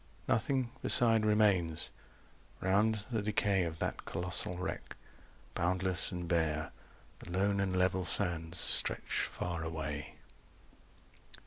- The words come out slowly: Yes, slow, 110 wpm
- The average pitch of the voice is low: Yes, very low, 90 Hz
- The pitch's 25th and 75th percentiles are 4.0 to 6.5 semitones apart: No, average, 3.3 semitones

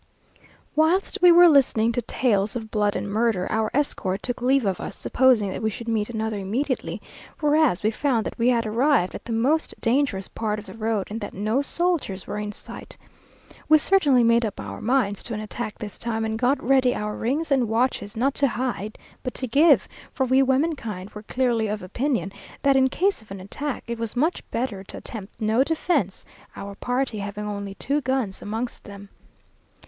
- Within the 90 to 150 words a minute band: No, average, 195 wpm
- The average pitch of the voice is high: Yes, high, 230 Hz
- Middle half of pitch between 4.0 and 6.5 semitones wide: Yes, average, 4.3 semitones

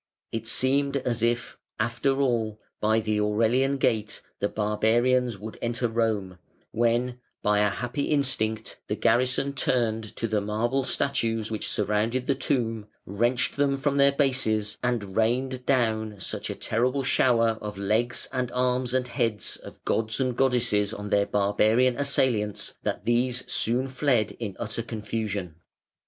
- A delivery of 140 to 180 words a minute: Yes, average, 145 wpm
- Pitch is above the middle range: No, low, 115 Hz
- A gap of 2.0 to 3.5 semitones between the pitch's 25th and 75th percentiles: Yes, average, 3.0 semitones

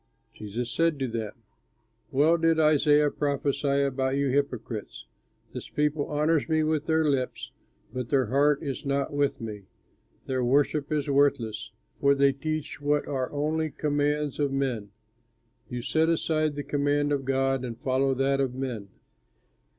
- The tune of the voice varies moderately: No, narrow, 2.1 semitones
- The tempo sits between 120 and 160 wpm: Yes, average, 150 wpm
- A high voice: No, medium, 140 Hz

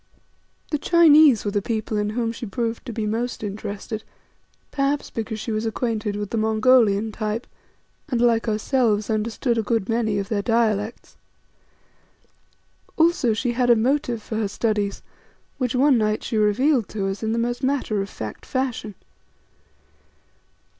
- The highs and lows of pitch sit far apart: No, narrow, 2.5 semitones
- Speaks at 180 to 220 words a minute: No, average, 155 wpm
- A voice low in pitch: No, high, 225 Hz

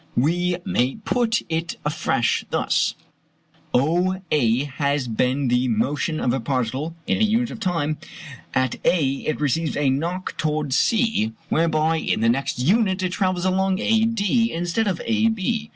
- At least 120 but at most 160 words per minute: Yes, average, 150 wpm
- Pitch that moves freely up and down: Yes, wide, 5.9 semitones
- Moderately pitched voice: Yes, medium, 165 Hz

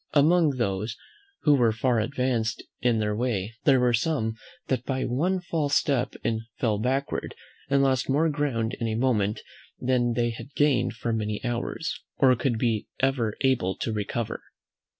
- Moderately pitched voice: No, low, 125 Hz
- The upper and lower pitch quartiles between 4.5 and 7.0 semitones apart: No, average, 3.3 semitones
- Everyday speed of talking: Yes, average, 160 wpm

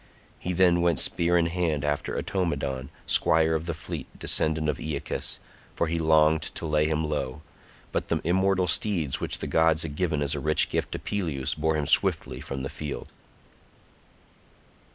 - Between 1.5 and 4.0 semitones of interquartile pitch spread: Yes, narrow, 2.4 semitones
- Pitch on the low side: Yes, very low, 80 Hz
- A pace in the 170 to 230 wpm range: Yes, average, 175 wpm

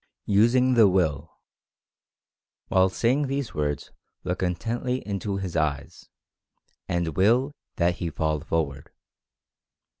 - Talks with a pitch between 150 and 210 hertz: No, very low, 95 Hz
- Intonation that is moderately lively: No, wide, 6.5 semitones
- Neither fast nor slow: No, slow, 110 wpm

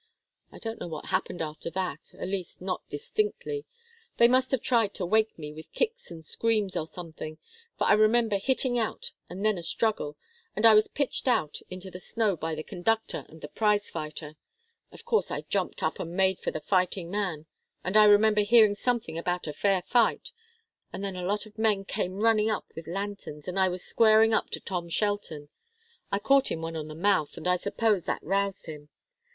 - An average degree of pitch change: Yes, average, 4.6 semitones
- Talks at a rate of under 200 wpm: No, fast, 205 wpm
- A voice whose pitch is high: Yes, high, 195 Hz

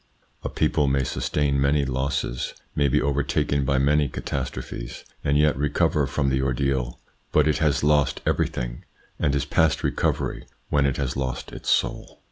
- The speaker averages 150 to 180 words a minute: Yes, average, 160 wpm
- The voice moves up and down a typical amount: No, narrow, 1.7 semitones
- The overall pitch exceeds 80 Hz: No, very low, 70 Hz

